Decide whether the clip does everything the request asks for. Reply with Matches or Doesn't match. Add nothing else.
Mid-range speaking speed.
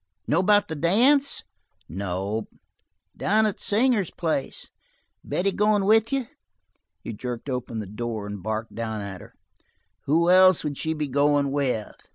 Matches